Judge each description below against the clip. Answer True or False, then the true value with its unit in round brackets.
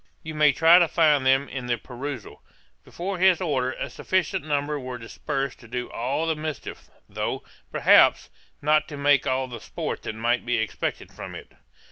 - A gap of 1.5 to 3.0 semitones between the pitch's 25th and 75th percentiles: False (3.7 semitones)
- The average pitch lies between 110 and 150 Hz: True (140 Hz)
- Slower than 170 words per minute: False (180 wpm)